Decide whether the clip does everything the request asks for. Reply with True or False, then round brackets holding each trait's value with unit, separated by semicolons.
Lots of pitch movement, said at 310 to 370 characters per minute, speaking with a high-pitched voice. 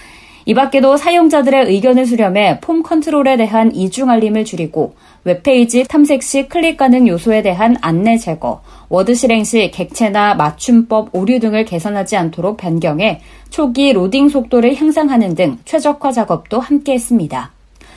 True (5.7 semitones; 330 characters per minute; 235 Hz)